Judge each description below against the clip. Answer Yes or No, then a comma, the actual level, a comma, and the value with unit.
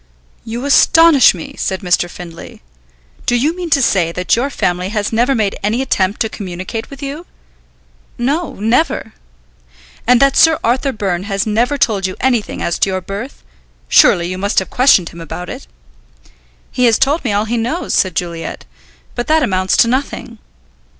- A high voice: Yes, high, 225 Hz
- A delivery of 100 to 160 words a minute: No, average, 175 wpm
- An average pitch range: No, wide, 6.1 semitones